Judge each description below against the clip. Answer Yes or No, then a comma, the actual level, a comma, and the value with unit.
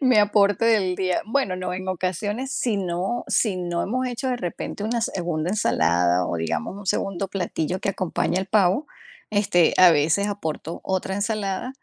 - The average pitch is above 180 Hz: Yes, high, 190 Hz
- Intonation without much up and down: No, average, 3.2 semitones